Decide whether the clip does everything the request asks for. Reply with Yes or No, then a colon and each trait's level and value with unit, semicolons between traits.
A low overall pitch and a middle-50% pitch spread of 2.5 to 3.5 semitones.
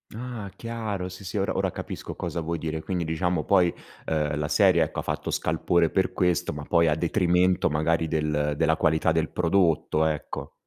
Yes: very low, 85 Hz; average, 2.8 semitones